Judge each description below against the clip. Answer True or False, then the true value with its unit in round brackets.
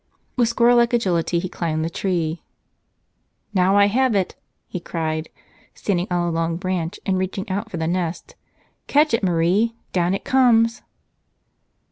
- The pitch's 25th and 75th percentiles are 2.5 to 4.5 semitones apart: False (5.0 semitones)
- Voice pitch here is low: False (185 Hz)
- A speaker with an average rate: True (155 wpm)